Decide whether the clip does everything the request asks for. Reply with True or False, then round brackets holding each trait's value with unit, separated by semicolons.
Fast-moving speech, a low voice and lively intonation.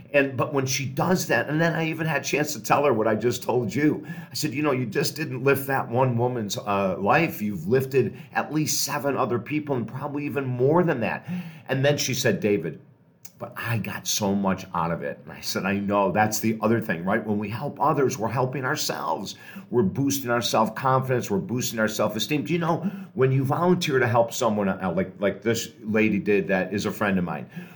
True (235 wpm; 130 Hz; 5.7 semitones)